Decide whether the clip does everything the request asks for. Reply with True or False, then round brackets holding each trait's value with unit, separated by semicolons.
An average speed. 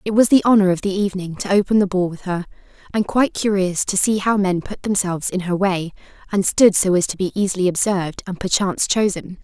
False (230 wpm)